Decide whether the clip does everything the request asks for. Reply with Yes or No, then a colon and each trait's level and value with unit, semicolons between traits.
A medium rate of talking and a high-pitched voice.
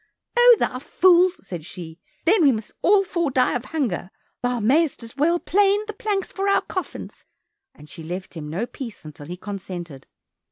Yes: average, 185 wpm; very high, 250 Hz